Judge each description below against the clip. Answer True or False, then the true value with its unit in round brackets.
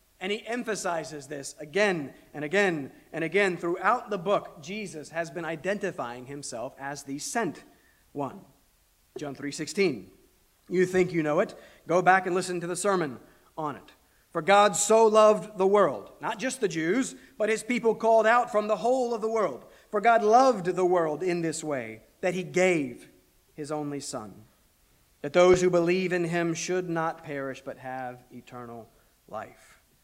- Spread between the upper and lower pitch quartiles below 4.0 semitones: False (5.4 semitones)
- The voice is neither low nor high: True (180 Hz)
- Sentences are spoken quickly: False (170 wpm)